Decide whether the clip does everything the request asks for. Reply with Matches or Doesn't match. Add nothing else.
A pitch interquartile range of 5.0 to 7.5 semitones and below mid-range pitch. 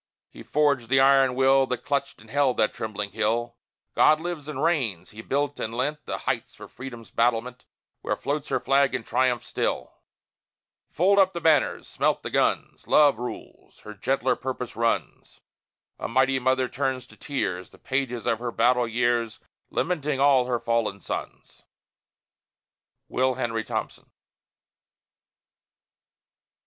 Doesn't match